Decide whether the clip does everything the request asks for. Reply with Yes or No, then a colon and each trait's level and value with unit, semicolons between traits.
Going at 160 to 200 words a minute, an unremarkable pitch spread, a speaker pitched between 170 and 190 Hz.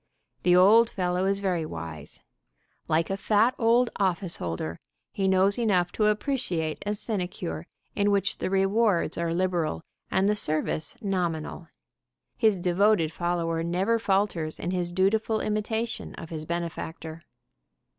No: slow, 135 wpm; average, 3.8 semitones; medium, 185 Hz